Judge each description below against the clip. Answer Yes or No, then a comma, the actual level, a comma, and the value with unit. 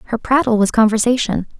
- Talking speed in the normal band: Yes, average, 150 wpm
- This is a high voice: Yes, high, 230 Hz